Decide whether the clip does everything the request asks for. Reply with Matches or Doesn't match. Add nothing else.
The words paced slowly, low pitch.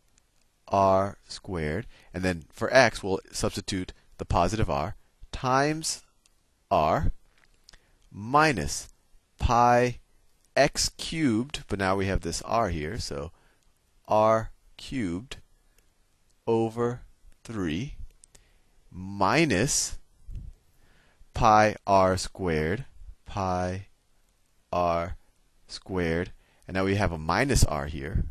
Matches